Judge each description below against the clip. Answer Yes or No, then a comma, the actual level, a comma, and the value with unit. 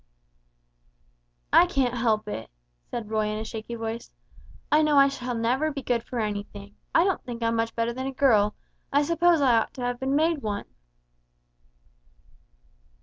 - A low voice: No, high, 240 Hz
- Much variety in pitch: No, average, 3.9 semitones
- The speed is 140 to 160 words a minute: No, average, 170 wpm